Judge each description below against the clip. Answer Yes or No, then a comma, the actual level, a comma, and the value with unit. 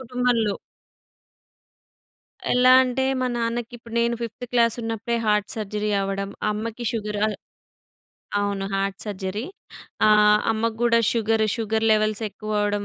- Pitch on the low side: No, high, 220 Hz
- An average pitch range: No, narrow, 2.0 semitones